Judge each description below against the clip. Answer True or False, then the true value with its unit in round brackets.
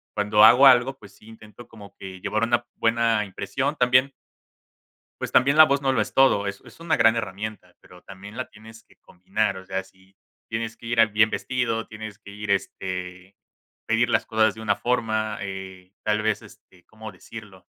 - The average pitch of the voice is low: True (110 Hz)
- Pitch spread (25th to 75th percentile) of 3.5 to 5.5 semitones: False (2.8 semitones)